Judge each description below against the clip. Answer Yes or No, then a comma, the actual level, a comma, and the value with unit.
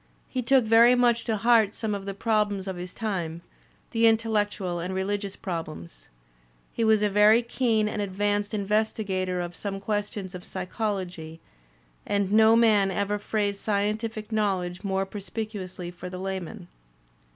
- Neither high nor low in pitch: No, high, 205 Hz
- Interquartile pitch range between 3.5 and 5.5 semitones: No, average, 2.7 semitones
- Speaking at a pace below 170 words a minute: Yes, average, 150 wpm